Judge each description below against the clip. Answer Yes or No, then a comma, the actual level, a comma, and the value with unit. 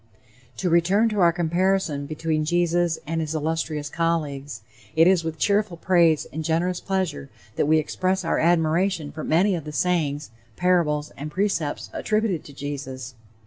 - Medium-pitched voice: Yes, medium, 165 Hz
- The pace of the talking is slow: No, average, 155 wpm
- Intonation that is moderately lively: Yes, average, 3.1 semitones